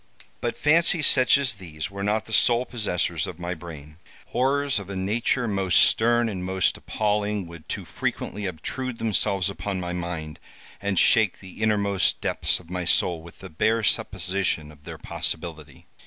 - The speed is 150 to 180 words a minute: Yes, average, 170 wpm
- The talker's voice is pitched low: Yes, low, 100 Hz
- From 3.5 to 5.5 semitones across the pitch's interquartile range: Yes, average, 4.3 semitones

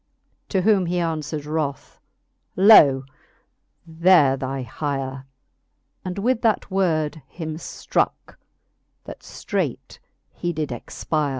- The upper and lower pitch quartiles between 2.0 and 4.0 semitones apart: No, average, 4.4 semitones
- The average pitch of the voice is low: No, medium, 160 Hz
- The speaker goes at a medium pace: No, slow, 100 wpm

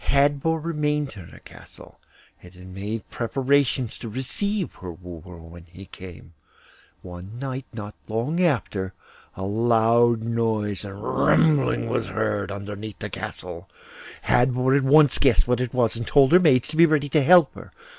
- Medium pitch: No, low, 115 Hz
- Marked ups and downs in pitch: Yes, wide, 5.9 semitones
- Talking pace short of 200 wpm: Yes, average, 160 wpm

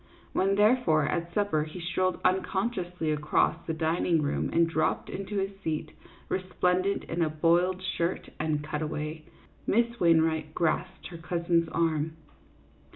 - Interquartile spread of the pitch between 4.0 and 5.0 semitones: No, average, 2.8 semitones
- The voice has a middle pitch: Yes, medium, 170 Hz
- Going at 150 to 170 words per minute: No, slow, 135 wpm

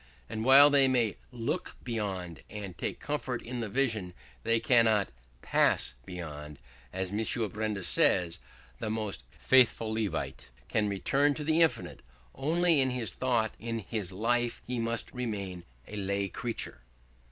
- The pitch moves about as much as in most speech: Yes, average, 4.1 semitones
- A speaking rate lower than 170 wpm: Yes, average, 145 wpm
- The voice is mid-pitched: No, low, 110 Hz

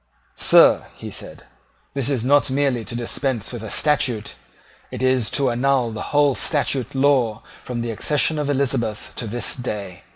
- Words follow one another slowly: No, average, 165 wpm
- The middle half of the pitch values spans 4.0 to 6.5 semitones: No, average, 3.2 semitones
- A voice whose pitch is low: Yes, low, 125 Hz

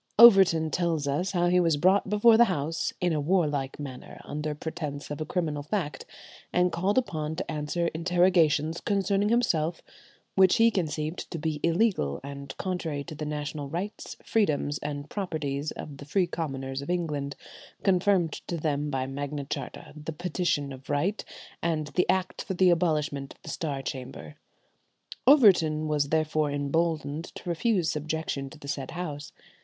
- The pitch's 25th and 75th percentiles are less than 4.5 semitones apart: Yes, average, 3.6 semitones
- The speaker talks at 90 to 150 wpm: No, average, 160 wpm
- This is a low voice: No, medium, 155 Hz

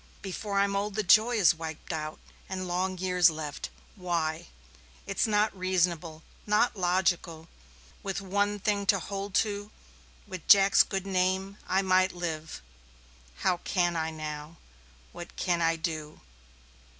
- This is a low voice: No, medium, 185 Hz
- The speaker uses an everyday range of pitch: Yes, average, 3.2 semitones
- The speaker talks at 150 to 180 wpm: No, average, 140 wpm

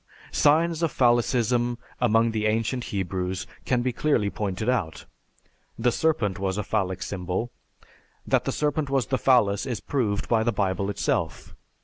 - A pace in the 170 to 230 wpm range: No, average, 150 wpm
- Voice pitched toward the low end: Yes, low, 115 Hz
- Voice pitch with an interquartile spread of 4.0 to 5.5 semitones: Yes, average, 4.3 semitones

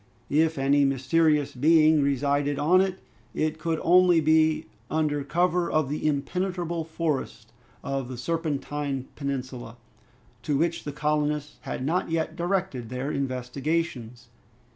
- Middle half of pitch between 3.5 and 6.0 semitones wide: No, average, 3.0 semitones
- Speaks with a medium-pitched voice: Yes, medium, 150 Hz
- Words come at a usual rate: No, slow, 125 wpm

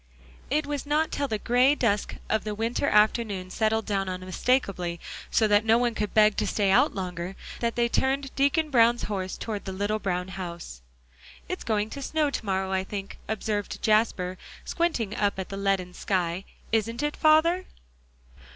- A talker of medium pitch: No, high, 215 Hz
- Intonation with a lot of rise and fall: No, average, 4.2 semitones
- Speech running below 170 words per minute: No, average, 175 wpm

